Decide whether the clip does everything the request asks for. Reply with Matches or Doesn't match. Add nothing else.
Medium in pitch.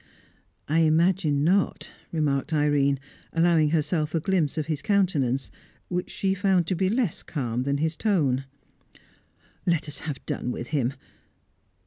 Matches